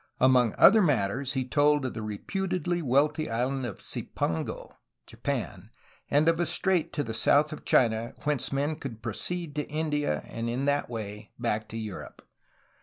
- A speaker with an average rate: Yes, average, 170 wpm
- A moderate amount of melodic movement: Yes, average, 4.9 semitones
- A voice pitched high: No, low, 135 Hz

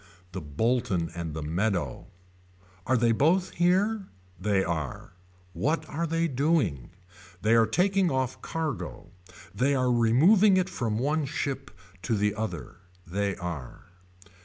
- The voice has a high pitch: No, low, 120 Hz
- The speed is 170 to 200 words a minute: No, slow, 135 wpm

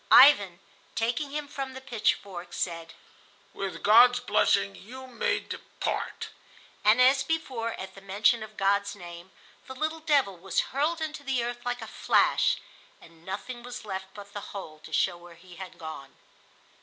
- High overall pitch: Yes, high, 215 Hz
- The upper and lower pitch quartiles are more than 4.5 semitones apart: Yes, wide, 5.6 semitones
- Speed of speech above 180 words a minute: No, average, 165 wpm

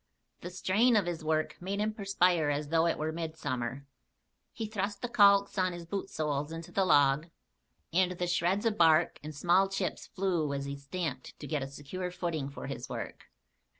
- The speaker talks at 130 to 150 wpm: No, average, 185 wpm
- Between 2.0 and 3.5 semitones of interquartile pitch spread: No, average, 4.2 semitones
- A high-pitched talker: No, medium, 170 Hz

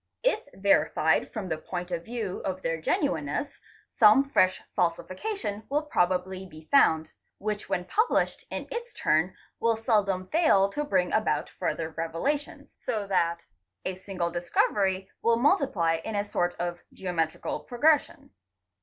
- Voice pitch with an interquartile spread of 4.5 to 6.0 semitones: Yes, average, 5.1 semitones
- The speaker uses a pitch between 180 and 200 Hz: Yes, high, 190 Hz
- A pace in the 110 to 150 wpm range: Yes, average, 140 wpm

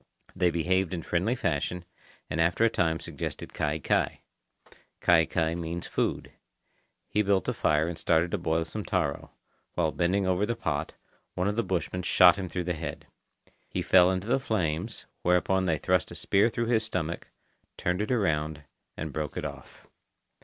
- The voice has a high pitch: No, very low, 90 Hz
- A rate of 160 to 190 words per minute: Yes, average, 175 wpm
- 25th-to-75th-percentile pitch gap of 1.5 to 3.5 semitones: Yes, average, 2.9 semitones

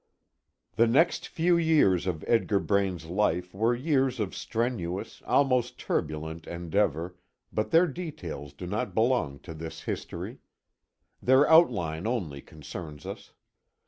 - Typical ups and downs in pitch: No, wide, 7.3 semitones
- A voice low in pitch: Yes, low, 100 Hz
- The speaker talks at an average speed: No, slow, 125 wpm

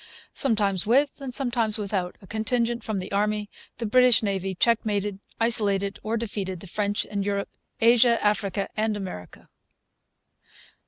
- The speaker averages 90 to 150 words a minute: Yes, average, 140 wpm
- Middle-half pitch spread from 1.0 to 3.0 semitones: Yes, average, 2.7 semitones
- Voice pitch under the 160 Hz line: No, high, 210 Hz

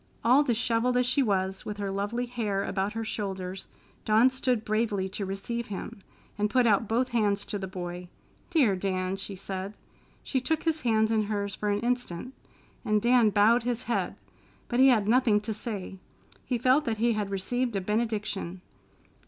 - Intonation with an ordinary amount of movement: Yes, average, 3.5 semitones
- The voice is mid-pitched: No, high, 215 Hz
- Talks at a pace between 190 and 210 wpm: No, average, 180 wpm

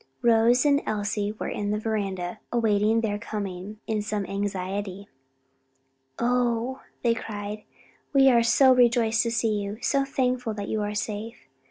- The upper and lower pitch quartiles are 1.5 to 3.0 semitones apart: Yes, narrow, 2.5 semitones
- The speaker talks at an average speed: Yes, average, 150 wpm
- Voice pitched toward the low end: No, high, 220 Hz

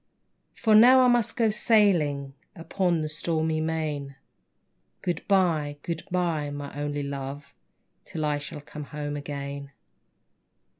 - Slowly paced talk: Yes, slow, 120 wpm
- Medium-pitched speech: Yes, medium, 155 Hz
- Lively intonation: No, average, 3.8 semitones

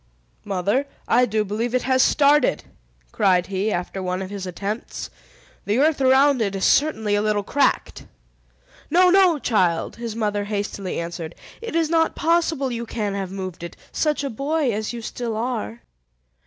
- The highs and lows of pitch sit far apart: Yes, wide, 6.0 semitones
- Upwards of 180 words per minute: No, average, 170 wpm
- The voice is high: Yes, high, 220 Hz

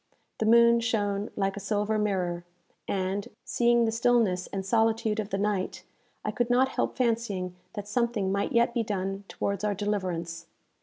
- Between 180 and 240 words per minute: No, average, 165 wpm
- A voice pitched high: Yes, high, 210 Hz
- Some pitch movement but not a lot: Yes, average, 3.0 semitones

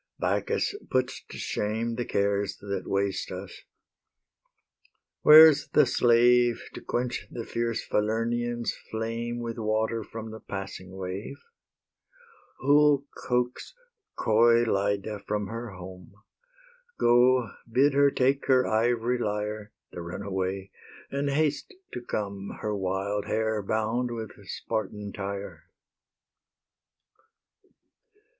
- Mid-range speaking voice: No, low, 110 Hz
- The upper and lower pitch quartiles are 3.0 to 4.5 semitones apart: Yes, average, 3.3 semitones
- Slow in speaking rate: Yes, slow, 110 wpm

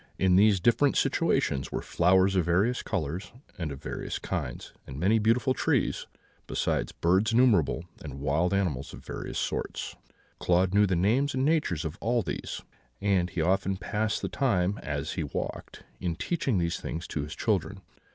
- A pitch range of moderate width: Yes, average, 4.5 semitones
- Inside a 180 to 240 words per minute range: No, average, 170 wpm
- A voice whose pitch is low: Yes, very low, 95 Hz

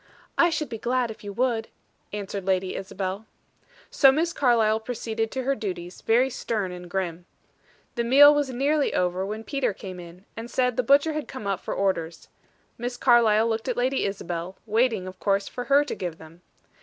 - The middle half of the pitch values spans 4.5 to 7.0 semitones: Yes, average, 5.0 semitones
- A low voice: No, high, 225 Hz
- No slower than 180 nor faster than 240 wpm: Yes, average, 190 wpm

